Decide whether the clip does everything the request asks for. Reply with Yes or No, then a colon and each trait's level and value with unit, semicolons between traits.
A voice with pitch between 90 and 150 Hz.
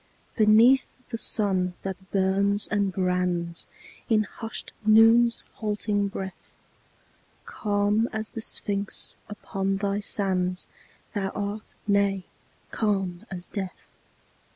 No: high, 200 Hz